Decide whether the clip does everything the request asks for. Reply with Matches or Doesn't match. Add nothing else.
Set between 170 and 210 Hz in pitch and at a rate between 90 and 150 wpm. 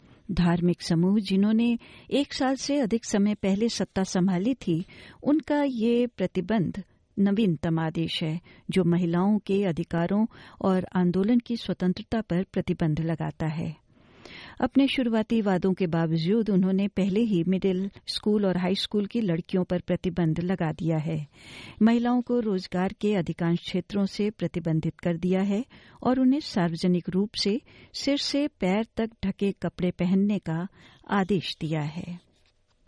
Matches